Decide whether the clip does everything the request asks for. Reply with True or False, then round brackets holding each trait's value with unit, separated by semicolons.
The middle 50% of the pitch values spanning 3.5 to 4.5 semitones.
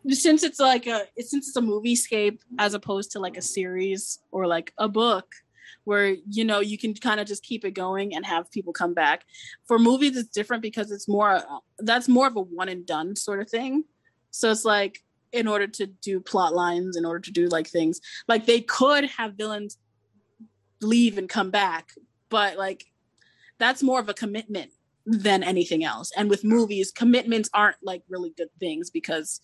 True (3.8 semitones)